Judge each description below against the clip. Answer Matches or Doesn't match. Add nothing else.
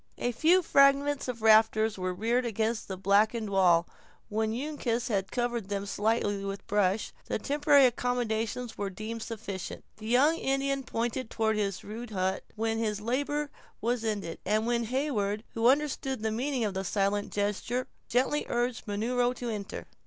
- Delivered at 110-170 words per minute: Matches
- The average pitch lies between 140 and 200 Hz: Doesn't match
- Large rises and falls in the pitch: Doesn't match